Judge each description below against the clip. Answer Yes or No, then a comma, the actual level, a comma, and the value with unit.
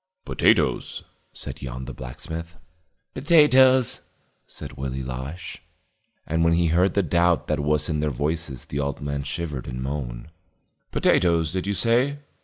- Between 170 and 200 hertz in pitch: No, very low, 80 Hz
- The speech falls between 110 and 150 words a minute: Yes, average, 145 wpm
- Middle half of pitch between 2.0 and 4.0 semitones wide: No, average, 4.4 semitones